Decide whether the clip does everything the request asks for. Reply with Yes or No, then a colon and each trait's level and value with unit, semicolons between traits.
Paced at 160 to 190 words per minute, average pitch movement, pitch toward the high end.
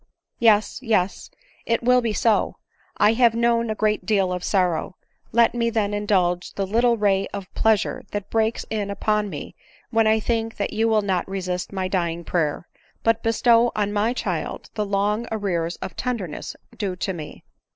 Yes: average, 185 wpm; average, 3.0 semitones; high, 210 Hz